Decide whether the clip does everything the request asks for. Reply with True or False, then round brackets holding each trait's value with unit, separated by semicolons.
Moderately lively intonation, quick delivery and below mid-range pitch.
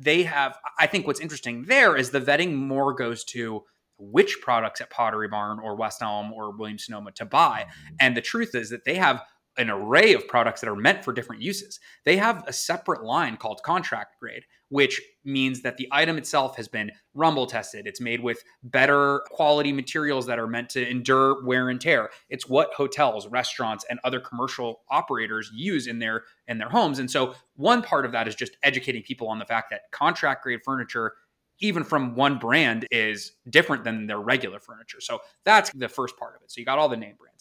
True (3.6 semitones; 210 wpm; 130 Hz)